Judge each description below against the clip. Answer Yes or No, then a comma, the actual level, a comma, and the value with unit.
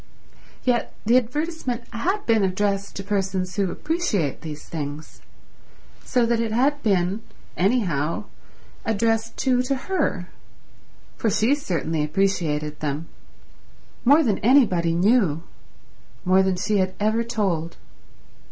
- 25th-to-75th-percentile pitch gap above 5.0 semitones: Yes, wide, 5.4 semitones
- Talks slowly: Yes, slow, 120 wpm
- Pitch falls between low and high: No, high, 205 Hz